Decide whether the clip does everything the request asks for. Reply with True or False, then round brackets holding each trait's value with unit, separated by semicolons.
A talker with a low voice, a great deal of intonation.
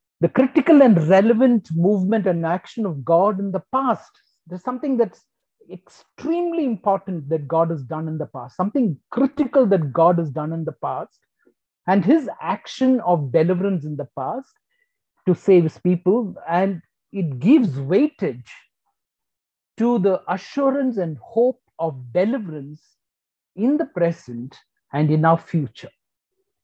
False (185 Hz; 7.5 semitones)